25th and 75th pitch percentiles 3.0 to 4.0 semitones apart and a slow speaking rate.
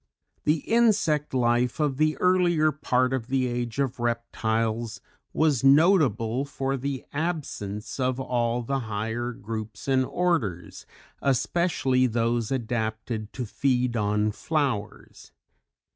Yes: average, 3.7 semitones; slow, 120 wpm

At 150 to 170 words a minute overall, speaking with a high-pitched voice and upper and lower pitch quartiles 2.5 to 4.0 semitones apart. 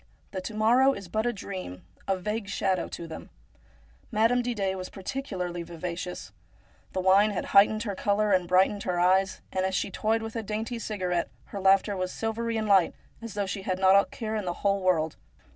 No: average, 200 wpm; high, 195 Hz; average, 2.8 semitones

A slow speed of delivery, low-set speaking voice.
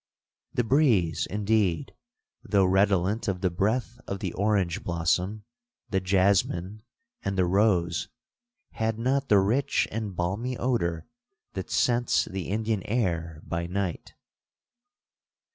Yes: slow, 120 wpm; low, 100 Hz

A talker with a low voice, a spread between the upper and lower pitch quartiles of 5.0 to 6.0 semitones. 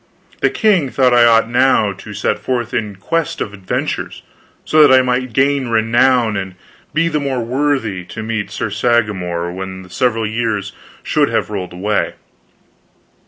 No: low, 115 Hz; average, 4.2 semitones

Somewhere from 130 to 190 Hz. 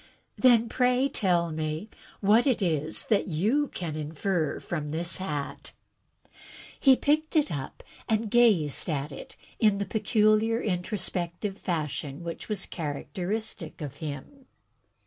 Yes: medium, 185 Hz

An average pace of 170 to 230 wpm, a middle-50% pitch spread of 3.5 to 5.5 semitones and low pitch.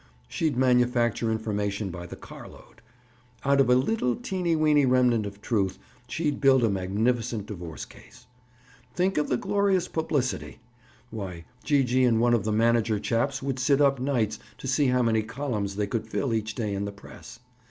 Yes: average, 180 wpm; average, 4.4 semitones; low, 120 Hz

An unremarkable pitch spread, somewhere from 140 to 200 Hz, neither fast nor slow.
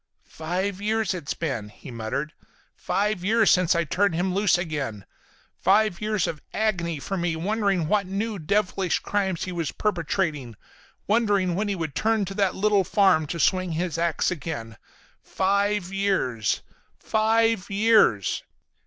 Yes: average, 3.9 semitones; high, 190 Hz; average, 145 wpm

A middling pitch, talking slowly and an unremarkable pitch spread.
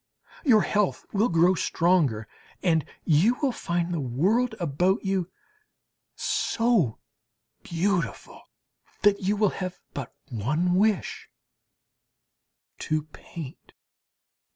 Yes: medium, 180 Hz; slow, 100 wpm; average, 4.4 semitones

